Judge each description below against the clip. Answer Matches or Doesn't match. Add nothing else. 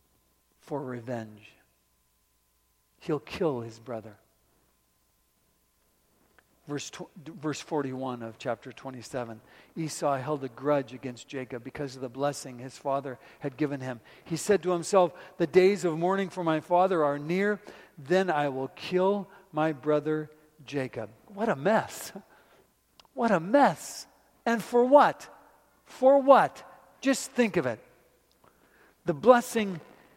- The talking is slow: Matches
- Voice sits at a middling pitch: Matches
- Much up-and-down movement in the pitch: Matches